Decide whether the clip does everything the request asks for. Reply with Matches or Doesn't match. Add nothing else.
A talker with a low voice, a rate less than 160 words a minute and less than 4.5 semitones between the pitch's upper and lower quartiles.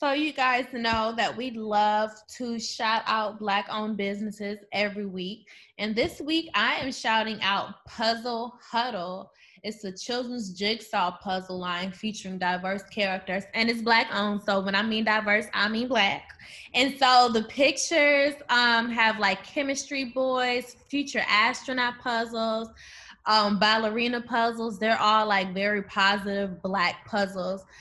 Doesn't match